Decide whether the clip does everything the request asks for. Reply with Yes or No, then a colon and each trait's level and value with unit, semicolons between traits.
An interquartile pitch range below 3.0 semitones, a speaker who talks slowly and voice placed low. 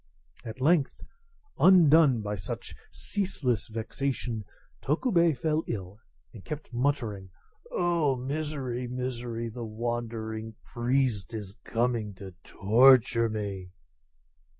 No: average, 4.2 semitones; slow, 100 wpm; low, 120 Hz